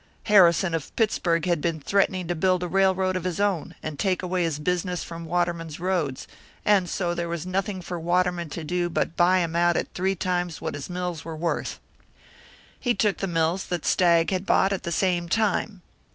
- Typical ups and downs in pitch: No, narrow, 1.8 semitones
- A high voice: No, medium, 175 Hz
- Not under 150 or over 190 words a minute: No, average, 200 wpm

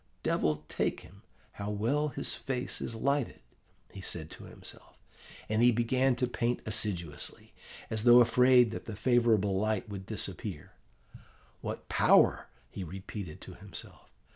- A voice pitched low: Yes, low, 110 Hz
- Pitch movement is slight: No, average, 4.1 semitones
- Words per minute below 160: Yes, average, 140 wpm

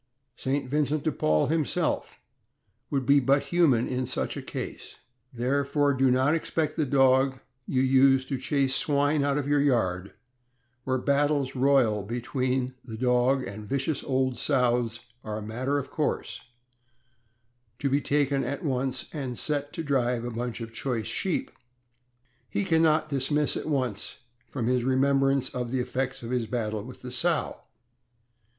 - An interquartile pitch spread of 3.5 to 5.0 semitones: No, narrow, 2.4 semitones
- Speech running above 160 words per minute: No, average, 155 wpm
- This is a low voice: Yes, low, 130 Hz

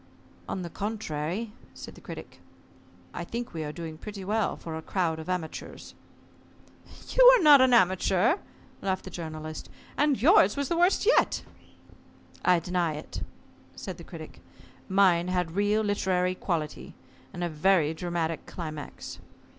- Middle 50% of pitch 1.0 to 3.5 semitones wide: No, average, 4.6 semitones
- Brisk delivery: No, average, 145 wpm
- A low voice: No, medium, 180 Hz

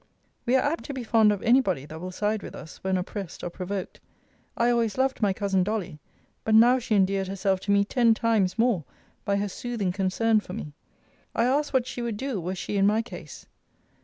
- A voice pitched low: No, high, 210 Hz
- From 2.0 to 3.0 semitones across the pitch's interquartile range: No, average, 3.8 semitones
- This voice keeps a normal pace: No, fast, 220 wpm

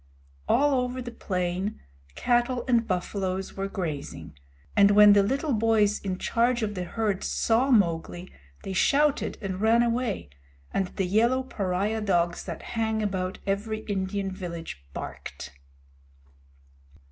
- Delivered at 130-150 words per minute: Yes, slow, 135 wpm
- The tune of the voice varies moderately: Yes, average, 3.9 semitones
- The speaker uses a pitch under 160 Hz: No, high, 205 Hz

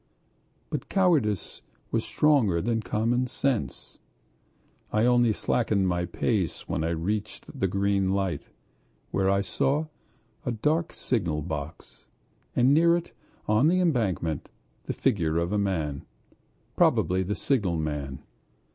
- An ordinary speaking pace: No, slow, 125 wpm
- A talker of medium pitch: No, low, 105 Hz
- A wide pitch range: Yes, wide, 6.1 semitones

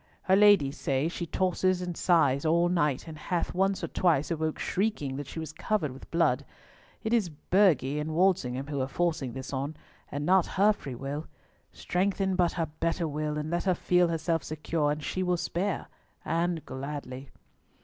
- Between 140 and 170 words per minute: No, average, 180 wpm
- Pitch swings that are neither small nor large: Yes, average, 3.7 semitones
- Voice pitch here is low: No, medium, 165 Hz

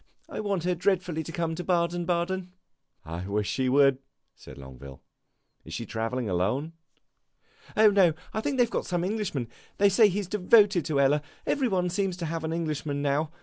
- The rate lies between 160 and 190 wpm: Yes, average, 185 wpm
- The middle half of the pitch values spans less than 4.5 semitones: No, wide, 5.5 semitones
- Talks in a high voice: No, medium, 170 Hz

